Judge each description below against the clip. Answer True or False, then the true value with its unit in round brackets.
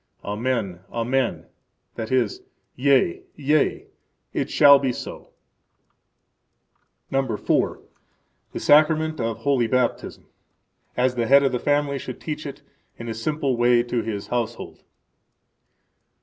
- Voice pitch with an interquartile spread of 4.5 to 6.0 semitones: False (3.2 semitones)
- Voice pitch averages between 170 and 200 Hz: False (130 Hz)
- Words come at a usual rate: False (115 wpm)